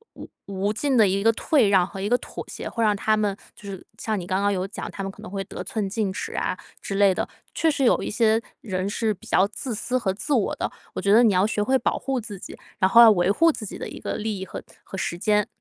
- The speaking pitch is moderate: No, high, 210 Hz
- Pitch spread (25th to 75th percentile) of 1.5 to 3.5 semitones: Yes, average, 2.7 semitones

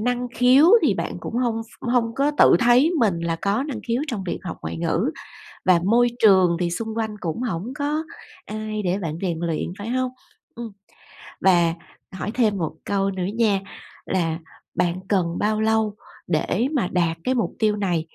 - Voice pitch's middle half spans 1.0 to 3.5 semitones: No, average, 5.1 semitones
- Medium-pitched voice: No, high, 210 Hz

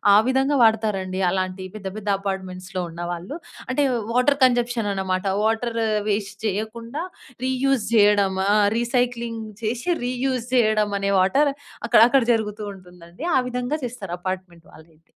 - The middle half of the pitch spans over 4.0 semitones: Yes, average, 4.5 semitones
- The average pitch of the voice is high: Yes, high, 215 Hz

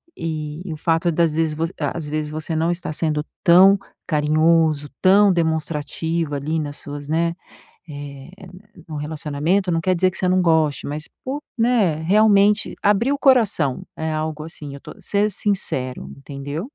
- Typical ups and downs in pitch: Yes, average, 3.6 semitones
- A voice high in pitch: No, medium, 160 Hz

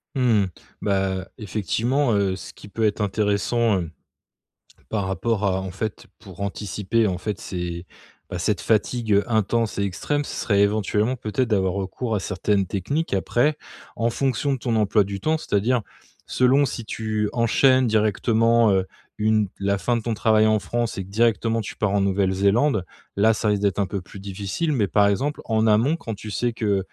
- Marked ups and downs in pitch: No, average, 2.9 semitones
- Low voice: Yes, low, 105 Hz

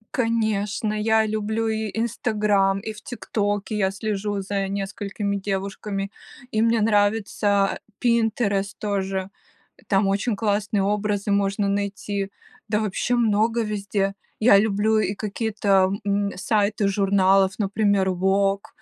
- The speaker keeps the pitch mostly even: Yes, narrow, 1.6 semitones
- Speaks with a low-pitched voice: No, high, 205 Hz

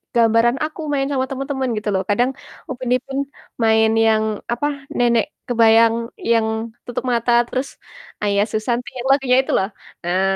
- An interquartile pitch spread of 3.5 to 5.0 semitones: No, average, 2.8 semitones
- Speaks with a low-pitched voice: No, high, 240 Hz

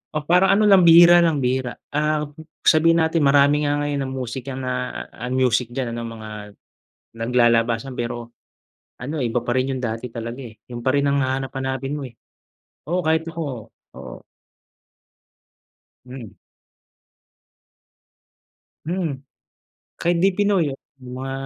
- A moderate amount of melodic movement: Yes, average, 4.1 semitones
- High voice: No, low, 135 Hz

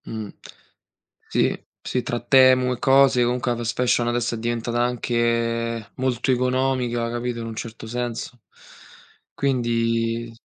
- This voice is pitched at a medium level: No, low, 120 Hz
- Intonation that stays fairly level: Yes, narrow, 1.3 semitones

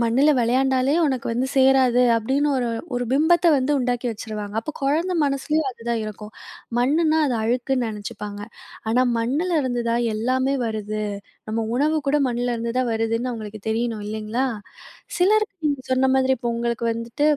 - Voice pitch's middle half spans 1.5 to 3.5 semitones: Yes, average, 3.1 semitones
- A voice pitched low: No, high, 245 Hz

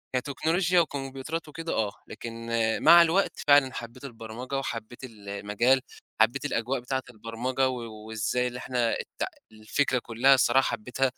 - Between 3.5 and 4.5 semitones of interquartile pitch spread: No, average, 3.0 semitones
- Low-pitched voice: Yes, low, 125 Hz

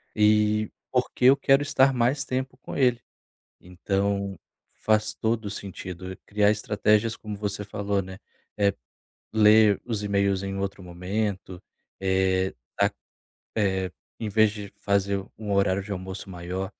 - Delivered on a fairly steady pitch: Yes, narrow, 2.2 semitones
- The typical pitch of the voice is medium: No, low, 100 Hz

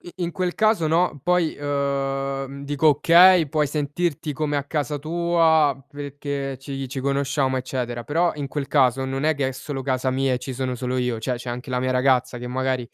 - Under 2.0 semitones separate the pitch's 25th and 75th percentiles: No, average, 2.7 semitones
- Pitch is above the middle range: No, medium, 140 Hz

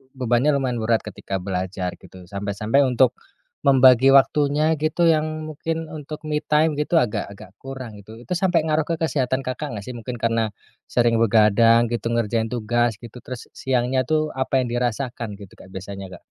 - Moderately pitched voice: No, low, 120 Hz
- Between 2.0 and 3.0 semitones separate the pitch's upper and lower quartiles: No, average, 4.4 semitones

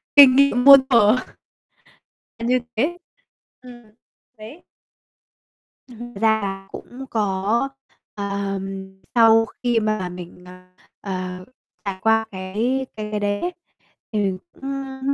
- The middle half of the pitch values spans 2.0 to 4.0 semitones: No, average, 4.5 semitones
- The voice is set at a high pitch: Yes, high, 215 Hz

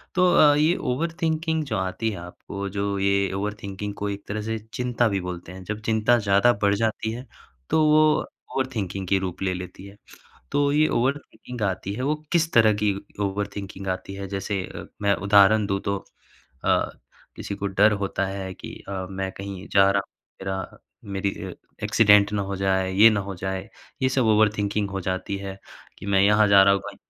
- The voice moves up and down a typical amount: No, narrow, 2.2 semitones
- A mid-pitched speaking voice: No, low, 100 Hz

